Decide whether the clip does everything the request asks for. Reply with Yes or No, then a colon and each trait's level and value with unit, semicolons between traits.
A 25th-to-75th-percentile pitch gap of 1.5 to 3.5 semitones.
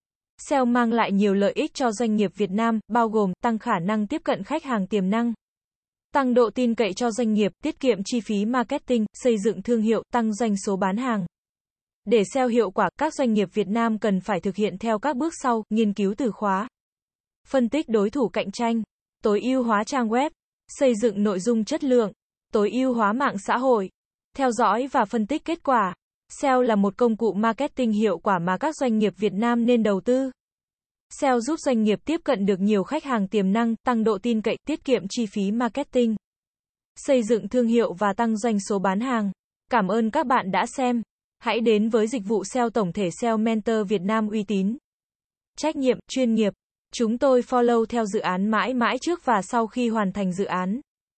Yes: average, 3.0 semitones